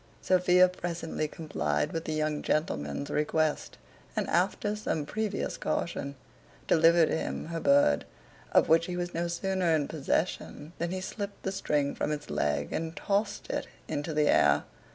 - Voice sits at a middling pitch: Yes, medium, 165 Hz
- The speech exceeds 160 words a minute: No, average, 155 wpm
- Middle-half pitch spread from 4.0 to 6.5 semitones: No, average, 3.3 semitones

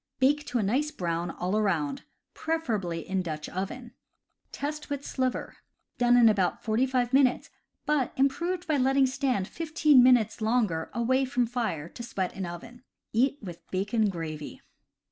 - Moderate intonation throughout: No, wide, 5.9 semitones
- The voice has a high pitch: Yes, high, 240 Hz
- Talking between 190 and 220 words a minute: No, average, 155 wpm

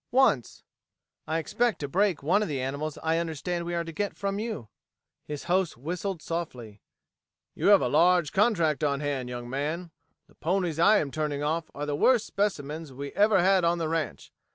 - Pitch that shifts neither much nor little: Yes, average, 4.7 semitones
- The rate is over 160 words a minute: Yes, average, 190 wpm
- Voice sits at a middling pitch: Yes, medium, 165 Hz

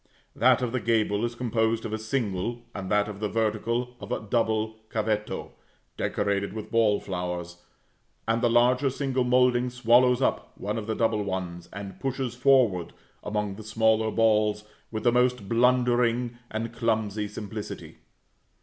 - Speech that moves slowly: No, average, 155 wpm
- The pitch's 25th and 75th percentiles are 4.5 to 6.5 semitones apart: No, narrow, 2.6 semitones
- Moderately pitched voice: No, low, 110 Hz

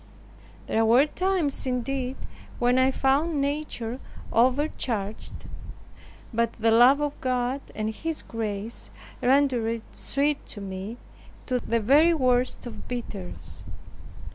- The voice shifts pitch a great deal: No, average, 3.7 semitones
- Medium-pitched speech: No, very high, 250 Hz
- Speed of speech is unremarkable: No, slow, 110 wpm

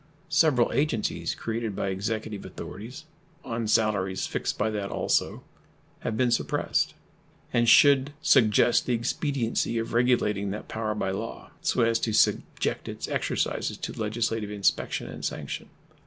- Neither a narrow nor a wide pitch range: No, narrow, 2.3 semitones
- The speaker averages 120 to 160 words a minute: Yes, average, 140 wpm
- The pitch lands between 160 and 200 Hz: No, low, 115 Hz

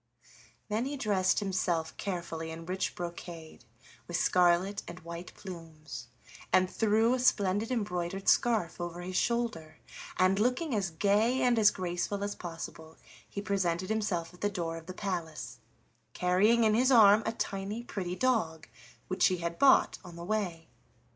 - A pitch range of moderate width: Yes, average, 3.8 semitones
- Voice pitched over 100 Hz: Yes, medium, 185 Hz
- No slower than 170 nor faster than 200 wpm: No, average, 155 wpm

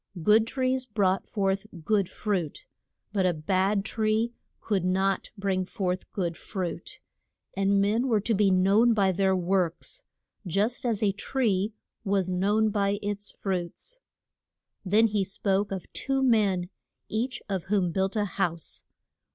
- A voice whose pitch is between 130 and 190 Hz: No, high, 200 Hz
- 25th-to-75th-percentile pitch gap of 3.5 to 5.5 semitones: No, narrow, 2.5 semitones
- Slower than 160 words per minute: Yes, average, 145 wpm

